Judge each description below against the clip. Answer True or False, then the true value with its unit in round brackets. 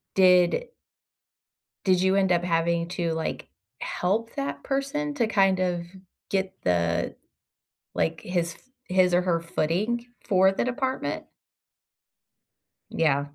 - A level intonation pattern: False (3.2 semitones)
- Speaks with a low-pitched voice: False (180 Hz)